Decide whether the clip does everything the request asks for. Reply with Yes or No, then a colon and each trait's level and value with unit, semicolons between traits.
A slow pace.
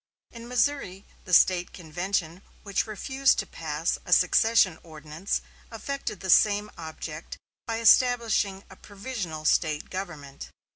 Yes: slow, 125 wpm